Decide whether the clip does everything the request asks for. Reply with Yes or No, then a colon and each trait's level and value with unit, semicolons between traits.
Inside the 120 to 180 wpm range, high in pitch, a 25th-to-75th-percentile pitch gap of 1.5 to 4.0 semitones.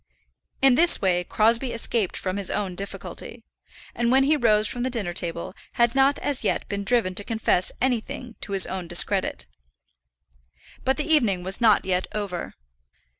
No: average, 170 wpm; high, 215 Hz; average, 4.6 semitones